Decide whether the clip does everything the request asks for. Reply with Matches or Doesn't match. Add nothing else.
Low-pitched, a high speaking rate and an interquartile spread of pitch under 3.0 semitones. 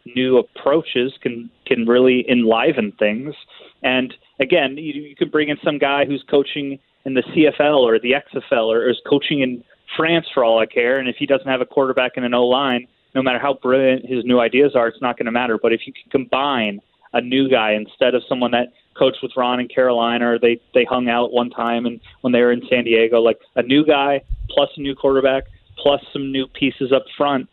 Matches